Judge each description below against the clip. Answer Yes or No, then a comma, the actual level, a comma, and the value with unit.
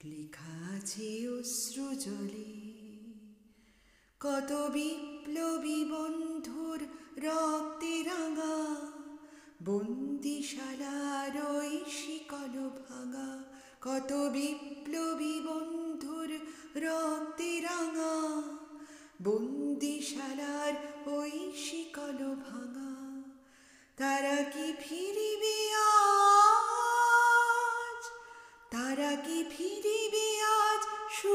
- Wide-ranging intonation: No, average, 3.1 semitones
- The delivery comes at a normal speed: Yes, average, 35 wpm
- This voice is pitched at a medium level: No, very high, 300 Hz